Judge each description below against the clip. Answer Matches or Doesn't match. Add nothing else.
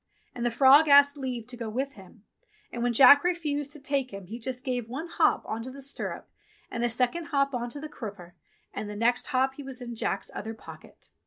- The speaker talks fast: Matches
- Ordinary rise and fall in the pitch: Matches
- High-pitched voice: Matches